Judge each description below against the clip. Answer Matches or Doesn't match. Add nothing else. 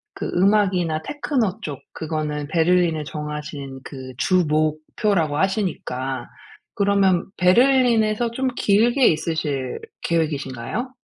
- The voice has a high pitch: Doesn't match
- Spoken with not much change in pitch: Doesn't match